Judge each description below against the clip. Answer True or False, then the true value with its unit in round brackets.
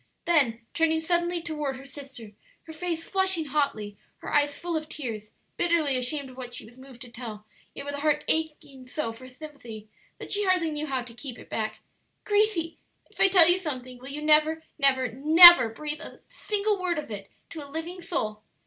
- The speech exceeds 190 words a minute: True (200 wpm)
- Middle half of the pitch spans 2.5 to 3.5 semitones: False (4.6 semitones)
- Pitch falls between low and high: False (295 Hz)